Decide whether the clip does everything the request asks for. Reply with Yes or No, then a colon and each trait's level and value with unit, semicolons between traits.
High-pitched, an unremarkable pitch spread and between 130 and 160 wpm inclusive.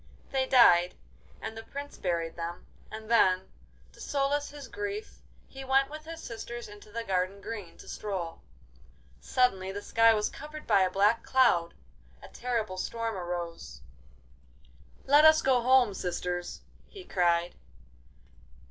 No: high, 220 Hz; wide, 6.6 semitones; average, 140 wpm